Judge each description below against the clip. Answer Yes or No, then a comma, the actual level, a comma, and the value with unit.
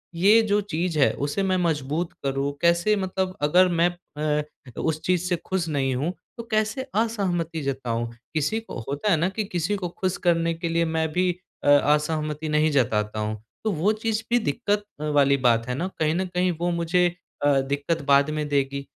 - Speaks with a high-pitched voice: No, medium, 165 Hz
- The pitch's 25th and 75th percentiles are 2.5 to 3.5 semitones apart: No, average, 4.4 semitones